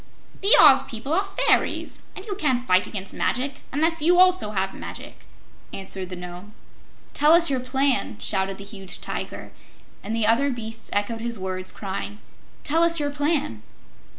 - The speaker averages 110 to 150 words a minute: No, average, 165 wpm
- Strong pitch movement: Yes, wide, 7.3 semitones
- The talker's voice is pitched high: Yes, high, 240 Hz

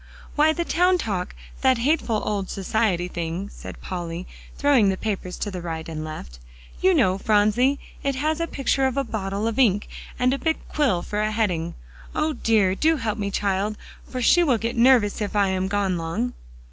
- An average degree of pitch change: No, wide, 5.8 semitones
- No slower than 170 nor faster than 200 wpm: Yes, average, 190 wpm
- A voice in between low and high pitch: No, high, 215 Hz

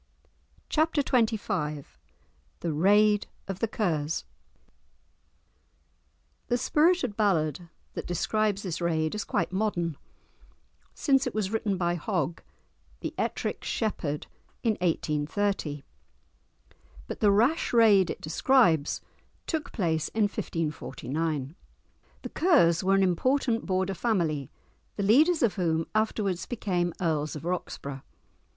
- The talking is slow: Yes, slow, 115 wpm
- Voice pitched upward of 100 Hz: Yes, high, 190 Hz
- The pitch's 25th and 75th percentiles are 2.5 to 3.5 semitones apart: No, average, 5.2 semitones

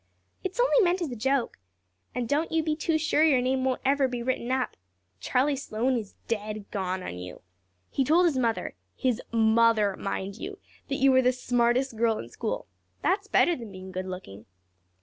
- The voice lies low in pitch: No, very high, 250 Hz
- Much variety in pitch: No, average, 4.7 semitones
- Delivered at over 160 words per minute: Yes, average, 190 wpm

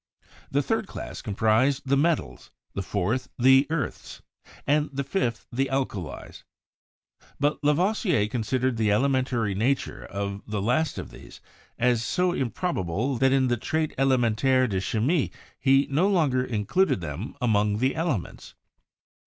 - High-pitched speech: No, low, 130 Hz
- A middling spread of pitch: Yes, average, 4.5 semitones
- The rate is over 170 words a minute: No, average, 145 wpm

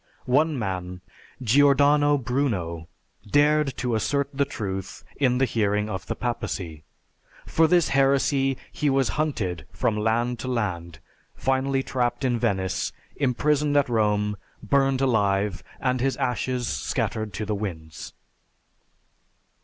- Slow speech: Yes, slow, 125 wpm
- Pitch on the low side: Yes, low, 125 Hz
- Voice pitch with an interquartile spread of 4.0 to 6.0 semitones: Yes, average, 4.9 semitones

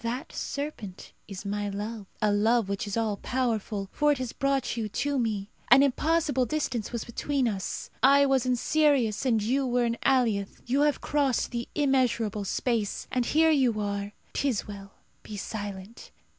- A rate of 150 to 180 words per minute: Yes, average, 170 wpm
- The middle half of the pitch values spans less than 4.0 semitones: No, average, 4.6 semitones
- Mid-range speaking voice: No, high, 235 Hz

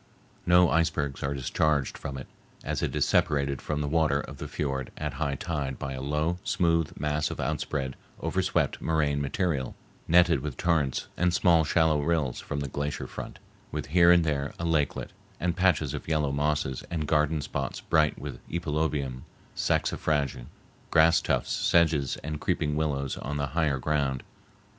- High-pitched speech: No, very low, 75 Hz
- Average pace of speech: Yes, average, 165 wpm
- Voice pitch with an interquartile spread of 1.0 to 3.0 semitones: Yes, narrow, 2.5 semitones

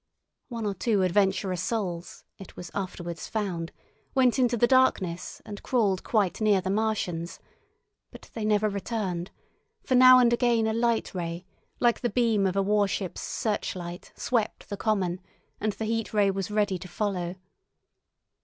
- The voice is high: Yes, high, 205 Hz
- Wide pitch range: No, average, 3.5 semitones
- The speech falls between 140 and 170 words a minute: Yes, average, 155 wpm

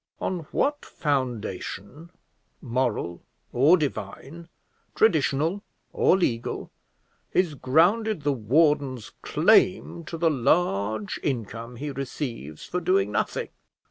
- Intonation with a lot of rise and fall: Yes, wide, 6.3 semitones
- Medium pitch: Yes, medium, 145 Hz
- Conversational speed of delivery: No, slow, 100 wpm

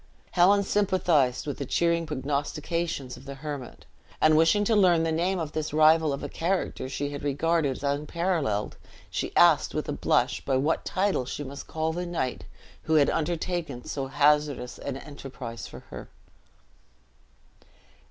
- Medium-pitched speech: Yes, medium, 150 Hz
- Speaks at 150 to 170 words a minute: Yes, average, 160 wpm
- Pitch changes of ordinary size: Yes, average, 3.4 semitones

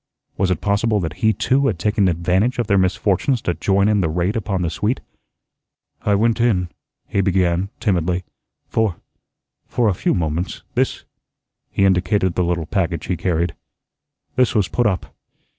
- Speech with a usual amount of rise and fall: Yes, average, 3.2 semitones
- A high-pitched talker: No, very low, 95 Hz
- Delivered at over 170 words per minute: No, average, 165 wpm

